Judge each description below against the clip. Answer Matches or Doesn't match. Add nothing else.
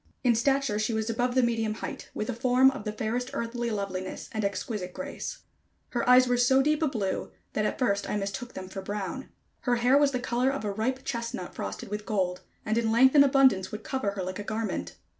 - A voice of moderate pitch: Doesn't match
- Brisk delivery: Matches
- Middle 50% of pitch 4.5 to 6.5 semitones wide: Doesn't match